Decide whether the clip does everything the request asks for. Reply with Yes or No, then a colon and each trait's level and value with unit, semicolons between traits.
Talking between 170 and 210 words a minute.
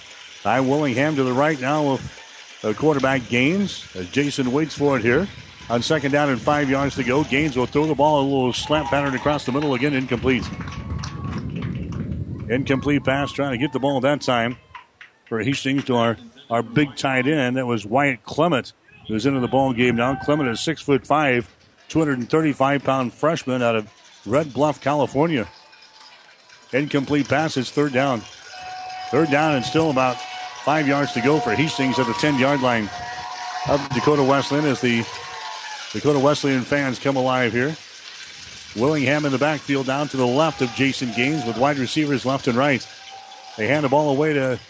Yes: average, 175 wpm